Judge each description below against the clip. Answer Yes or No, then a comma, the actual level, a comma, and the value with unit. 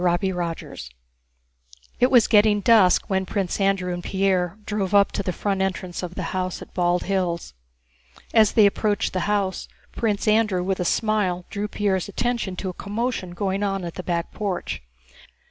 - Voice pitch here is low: No, high, 195 Hz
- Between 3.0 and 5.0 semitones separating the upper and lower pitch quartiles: No, narrow, 2.5 semitones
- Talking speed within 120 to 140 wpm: No, average, 175 wpm